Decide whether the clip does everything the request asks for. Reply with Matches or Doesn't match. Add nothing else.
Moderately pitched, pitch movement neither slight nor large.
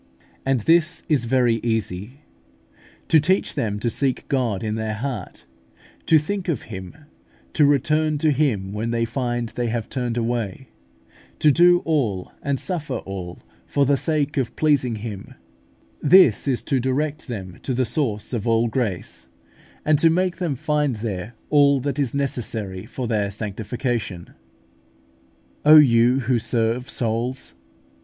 Doesn't match